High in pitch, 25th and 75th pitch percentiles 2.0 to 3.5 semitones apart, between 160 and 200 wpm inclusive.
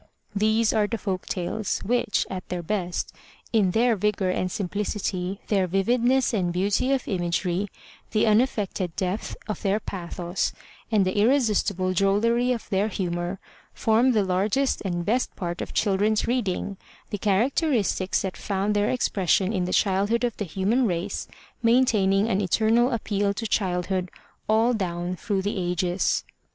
No: high, 200 Hz; average, 3.2 semitones; average, 150 wpm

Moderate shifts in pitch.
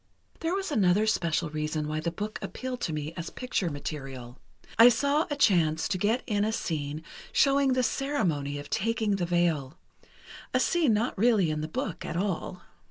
No: wide, 7.5 semitones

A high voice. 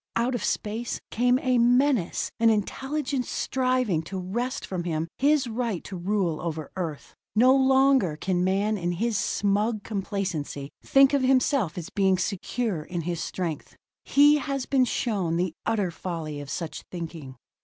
Yes: high, 205 Hz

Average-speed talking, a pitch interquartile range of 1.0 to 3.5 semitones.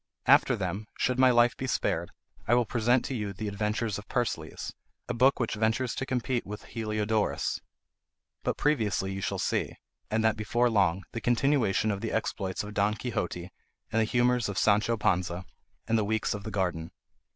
Yes: average, 185 wpm; average, 3.0 semitones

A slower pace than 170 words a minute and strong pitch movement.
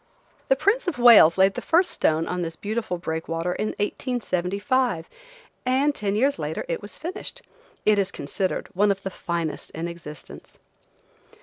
Yes: average, 160 wpm; wide, 6.6 semitones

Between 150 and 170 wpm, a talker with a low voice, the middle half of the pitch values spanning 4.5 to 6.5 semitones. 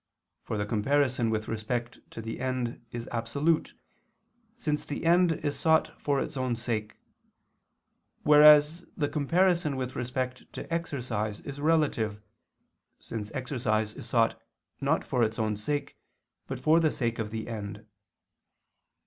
No: average, 140 wpm; low, 125 Hz; average, 4.9 semitones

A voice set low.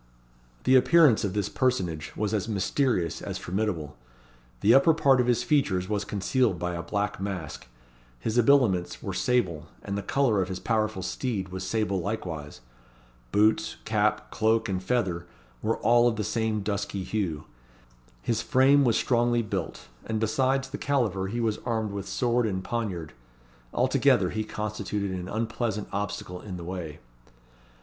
Yes: low, 105 Hz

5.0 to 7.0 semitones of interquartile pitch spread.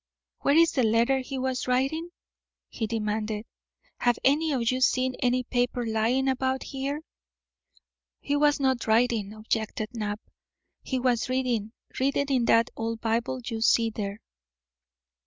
No: average, 2.9 semitones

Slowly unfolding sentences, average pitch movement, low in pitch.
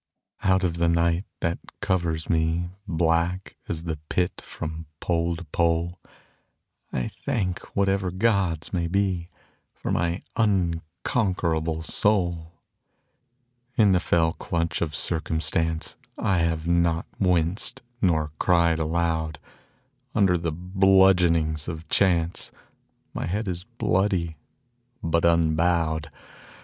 No: slow, 110 wpm; narrow, 2.0 semitones; very low, 85 Hz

